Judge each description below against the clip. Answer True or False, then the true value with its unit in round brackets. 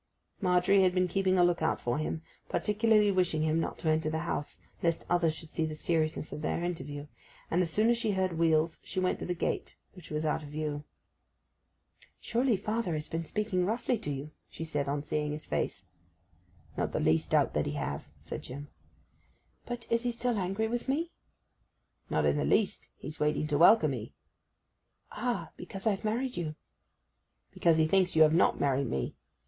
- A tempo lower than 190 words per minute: False (195 wpm)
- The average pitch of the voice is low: False (170 Hz)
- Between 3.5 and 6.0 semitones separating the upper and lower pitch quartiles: True (4.7 semitones)